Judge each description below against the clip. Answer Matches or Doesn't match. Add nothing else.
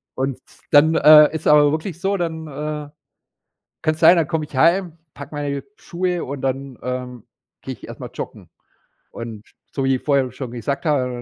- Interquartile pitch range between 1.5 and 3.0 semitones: Doesn't match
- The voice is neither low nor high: Matches